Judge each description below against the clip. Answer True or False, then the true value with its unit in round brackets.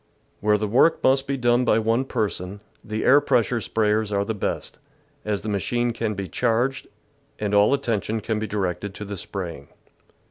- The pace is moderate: True (180 wpm)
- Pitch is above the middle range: False (110 Hz)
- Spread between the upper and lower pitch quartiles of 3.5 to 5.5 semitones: False (2.8 semitones)